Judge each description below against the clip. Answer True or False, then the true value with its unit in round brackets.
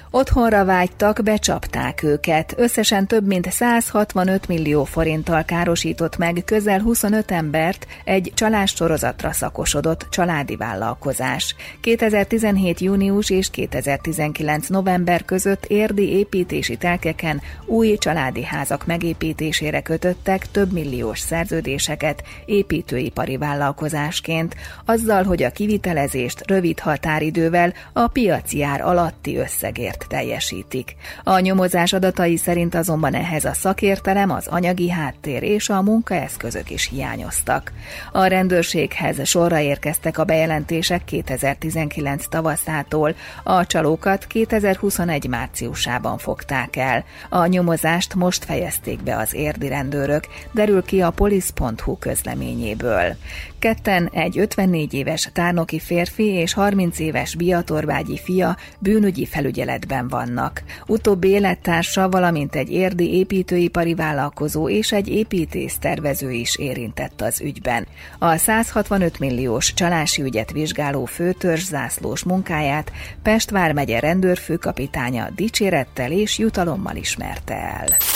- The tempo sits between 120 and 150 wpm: False (105 wpm)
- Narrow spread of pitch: False (4.2 semitones)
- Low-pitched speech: False (170 Hz)